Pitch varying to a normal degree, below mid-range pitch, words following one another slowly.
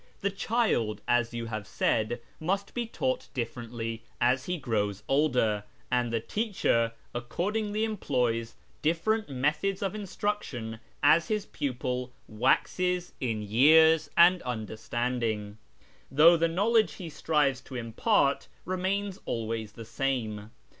No: wide, 7.8 semitones; low, 130 Hz; slow, 125 wpm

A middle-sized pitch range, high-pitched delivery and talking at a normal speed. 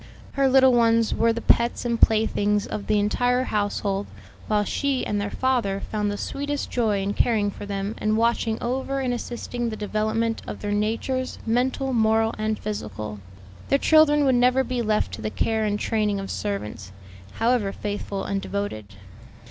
Yes: average, 3.2 semitones; high, 220 Hz; average, 170 wpm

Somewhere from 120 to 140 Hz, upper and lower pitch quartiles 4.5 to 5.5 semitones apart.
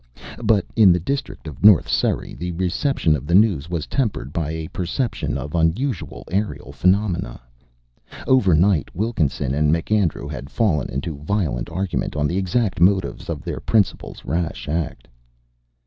No: very low, 85 Hz; average, 5.0 semitones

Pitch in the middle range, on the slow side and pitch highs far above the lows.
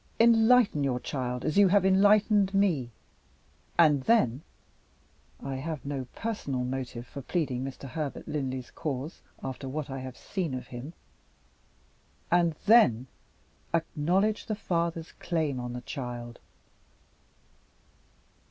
Yes: medium, 150 Hz; slow, 120 wpm; wide, 6.5 semitones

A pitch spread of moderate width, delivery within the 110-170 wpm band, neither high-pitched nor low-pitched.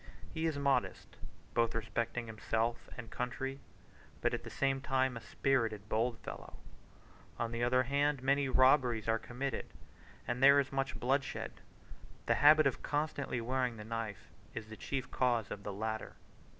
No: average, 3.0 semitones; average, 160 wpm; low, 125 Hz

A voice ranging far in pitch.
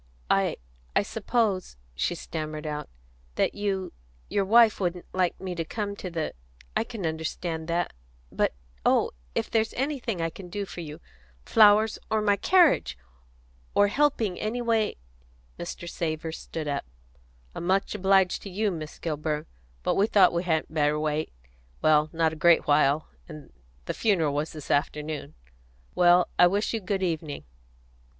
No: average, 4.7 semitones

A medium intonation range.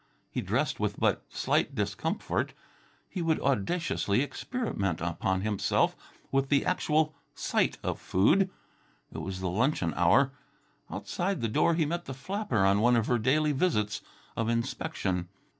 No: wide, 8.2 semitones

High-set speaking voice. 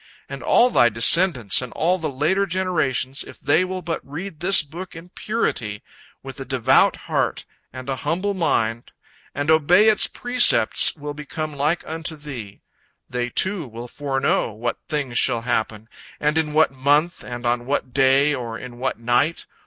No: medium, 145 Hz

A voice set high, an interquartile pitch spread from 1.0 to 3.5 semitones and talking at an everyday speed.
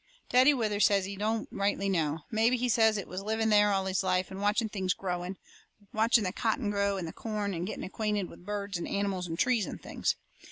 No: high, 200 Hz; narrow, 2.6 semitones; fast, 220 wpm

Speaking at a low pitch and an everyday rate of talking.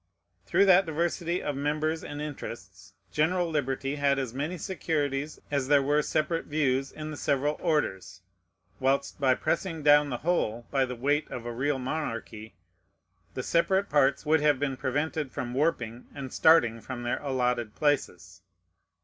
No: medium, 145 Hz; average, 160 wpm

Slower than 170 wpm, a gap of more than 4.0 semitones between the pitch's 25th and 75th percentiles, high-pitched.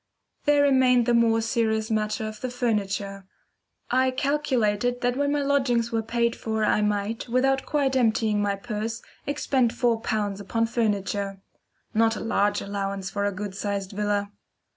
No: average, 160 wpm; average, 3.2 semitones; high, 225 Hz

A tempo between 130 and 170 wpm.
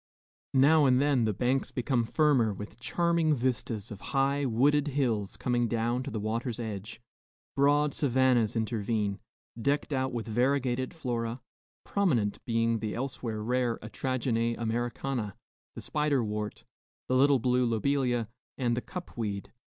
Yes: average, 140 wpm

